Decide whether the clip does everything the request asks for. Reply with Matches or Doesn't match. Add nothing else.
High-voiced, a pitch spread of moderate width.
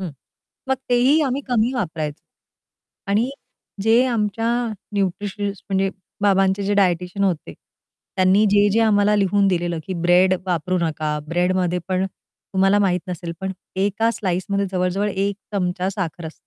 Doesn't match